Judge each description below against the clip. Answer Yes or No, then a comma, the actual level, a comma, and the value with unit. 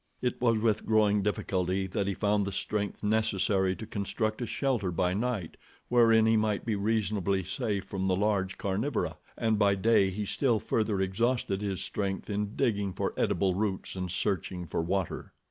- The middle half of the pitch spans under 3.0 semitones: Yes, narrow, 2.4 semitones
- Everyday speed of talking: Yes, average, 175 wpm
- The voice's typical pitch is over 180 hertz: No, low, 100 Hz